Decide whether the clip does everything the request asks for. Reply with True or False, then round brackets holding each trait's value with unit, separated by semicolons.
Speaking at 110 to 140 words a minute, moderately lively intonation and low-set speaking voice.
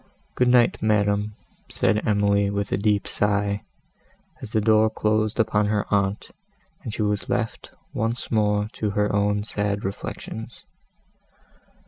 False (135 wpm; 1.1 semitones; 105 Hz)